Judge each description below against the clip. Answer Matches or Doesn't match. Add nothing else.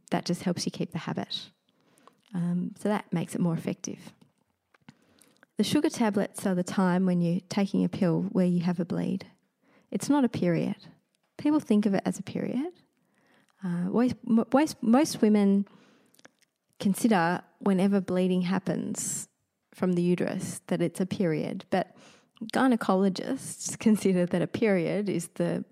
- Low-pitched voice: Doesn't match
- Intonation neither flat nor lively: Matches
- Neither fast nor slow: Matches